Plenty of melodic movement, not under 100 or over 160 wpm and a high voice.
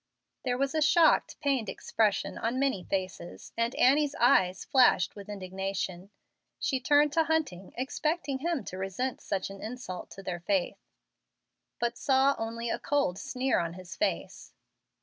Yes: wide, 6.4 semitones; average, 150 wpm; high, 235 Hz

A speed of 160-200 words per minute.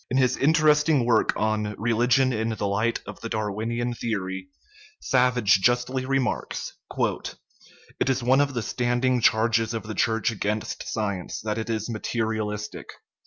No: average, 150 wpm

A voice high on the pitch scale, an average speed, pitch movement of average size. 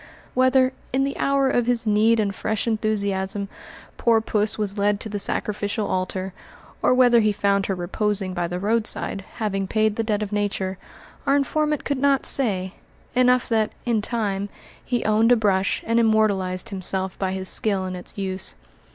Yes: high, 210 Hz; average, 175 wpm; average, 3.1 semitones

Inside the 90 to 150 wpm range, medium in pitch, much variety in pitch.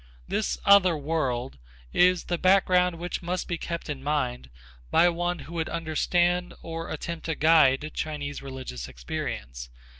No: average, 145 wpm; medium, 165 Hz; average, 4.2 semitones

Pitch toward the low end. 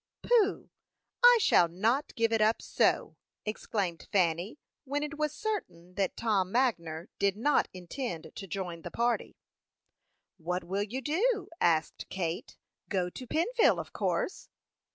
No: high, 210 Hz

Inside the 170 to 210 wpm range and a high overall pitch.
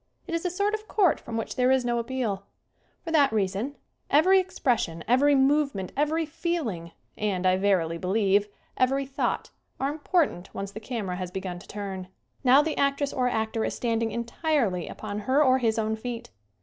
Yes: average, 185 wpm; high, 235 Hz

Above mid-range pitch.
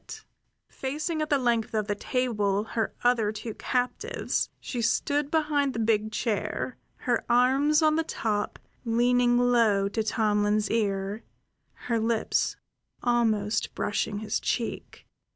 Yes: high, 230 Hz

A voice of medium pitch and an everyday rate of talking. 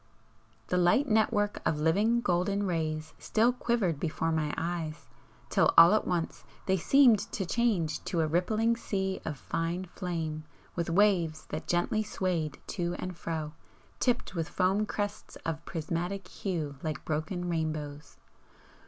Yes: medium, 175 Hz; average, 145 wpm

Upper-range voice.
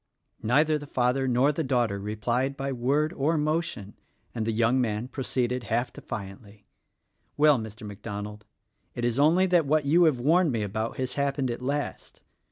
No: low, 125 Hz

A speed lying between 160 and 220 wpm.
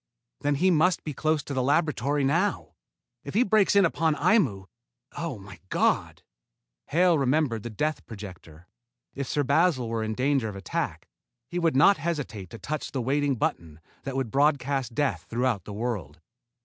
Yes: average, 170 wpm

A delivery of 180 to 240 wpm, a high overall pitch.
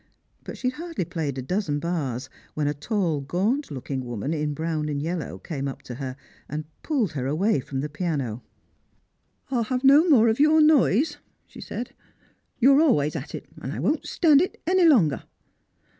No: average, 190 wpm; medium, 165 Hz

